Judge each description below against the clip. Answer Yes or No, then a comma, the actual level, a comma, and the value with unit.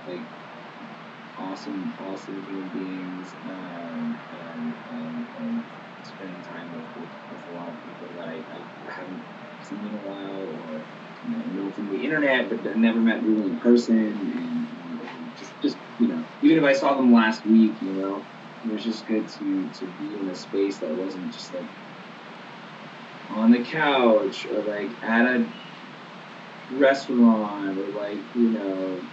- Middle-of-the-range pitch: No, low, 115 Hz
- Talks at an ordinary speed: Yes, average, 165 wpm